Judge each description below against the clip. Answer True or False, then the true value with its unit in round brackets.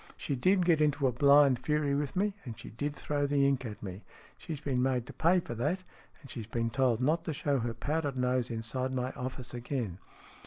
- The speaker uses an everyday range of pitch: True (3.2 semitones)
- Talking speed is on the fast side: True (220 wpm)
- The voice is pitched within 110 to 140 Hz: True (135 Hz)